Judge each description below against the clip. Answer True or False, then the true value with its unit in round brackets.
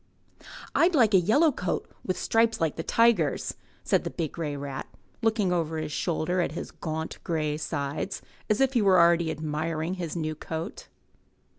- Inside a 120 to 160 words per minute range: False (170 wpm)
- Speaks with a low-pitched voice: False (170 Hz)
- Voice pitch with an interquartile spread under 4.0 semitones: False (4.6 semitones)